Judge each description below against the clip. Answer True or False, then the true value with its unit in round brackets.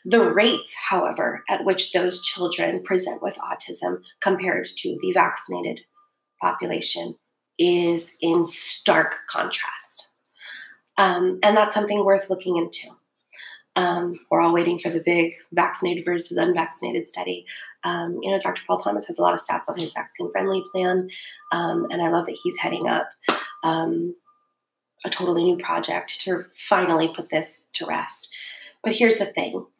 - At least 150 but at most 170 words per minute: True (155 wpm)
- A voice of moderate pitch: True (180 Hz)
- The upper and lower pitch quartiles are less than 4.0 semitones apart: True (2.7 semitones)